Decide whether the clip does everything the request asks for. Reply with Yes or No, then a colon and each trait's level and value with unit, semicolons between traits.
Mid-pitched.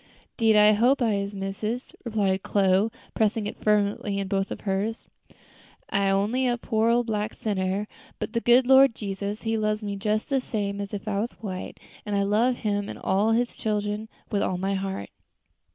No: high, 210 Hz